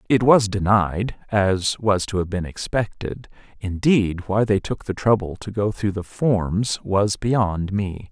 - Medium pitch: No, low, 100 Hz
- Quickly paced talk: No, average, 170 wpm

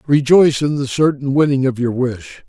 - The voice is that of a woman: No, male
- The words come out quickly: No, average, 195 wpm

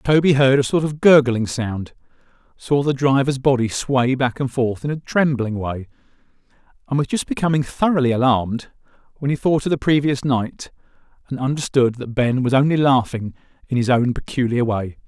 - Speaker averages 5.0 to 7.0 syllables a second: Yes, 5.2 syllables/s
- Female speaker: No, male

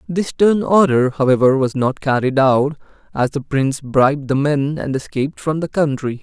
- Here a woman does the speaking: No, male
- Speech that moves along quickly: No, average, 185 wpm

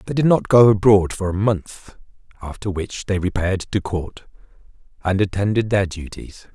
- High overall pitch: No, low, 100 Hz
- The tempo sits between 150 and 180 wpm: Yes, average, 165 wpm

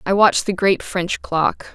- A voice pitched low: No, medium, 185 Hz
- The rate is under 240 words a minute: Yes, fast, 205 wpm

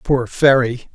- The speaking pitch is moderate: No, low, 125 Hz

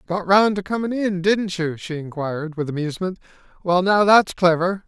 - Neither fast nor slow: Yes, average, 185 wpm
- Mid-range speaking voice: Yes, medium, 180 Hz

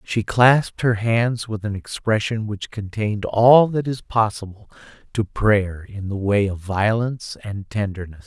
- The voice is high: No, low, 105 Hz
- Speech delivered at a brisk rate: No, average, 160 wpm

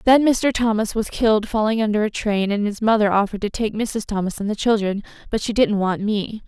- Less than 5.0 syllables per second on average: No, 5.6 syllables/s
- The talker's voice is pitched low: No, high, 210 Hz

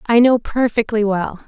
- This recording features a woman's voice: Yes, female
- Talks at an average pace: Yes, average, 165 wpm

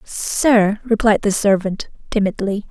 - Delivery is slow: Yes, slow, 110 wpm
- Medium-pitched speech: No, high, 205 Hz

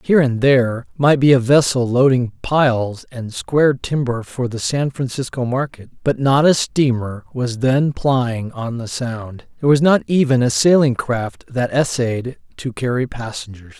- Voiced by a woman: No, male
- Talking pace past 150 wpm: Yes, average, 170 wpm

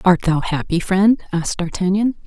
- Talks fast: No, average, 160 wpm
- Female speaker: Yes, female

